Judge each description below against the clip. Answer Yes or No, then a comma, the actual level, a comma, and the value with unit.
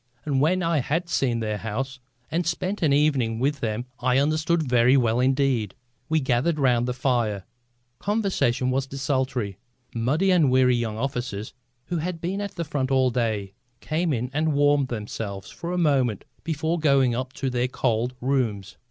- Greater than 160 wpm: Yes, average, 170 wpm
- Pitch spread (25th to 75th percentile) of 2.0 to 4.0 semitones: No, average, 4.5 semitones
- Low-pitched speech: Yes, low, 130 Hz